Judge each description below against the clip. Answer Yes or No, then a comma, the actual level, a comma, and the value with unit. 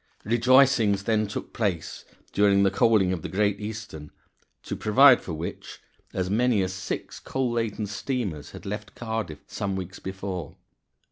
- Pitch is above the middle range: No, low, 105 Hz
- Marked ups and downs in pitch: No, average, 3.1 semitones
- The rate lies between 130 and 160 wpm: Yes, average, 150 wpm